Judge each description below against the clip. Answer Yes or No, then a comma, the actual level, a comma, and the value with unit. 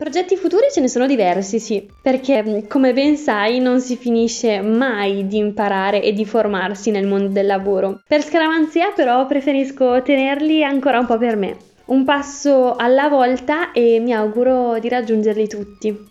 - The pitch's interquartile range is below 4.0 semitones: No, average, 4.6 semitones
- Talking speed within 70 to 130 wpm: No, average, 165 wpm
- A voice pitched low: No, high, 245 Hz